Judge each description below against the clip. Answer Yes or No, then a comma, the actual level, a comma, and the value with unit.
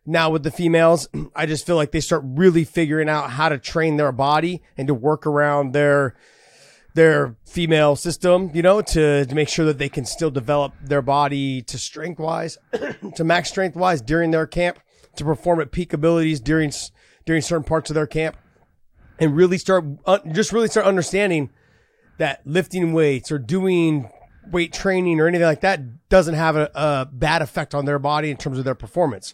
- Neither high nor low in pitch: Yes, medium, 160 Hz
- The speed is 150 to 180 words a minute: No, average, 190 wpm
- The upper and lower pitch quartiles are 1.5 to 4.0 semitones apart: Yes, average, 2.8 semitones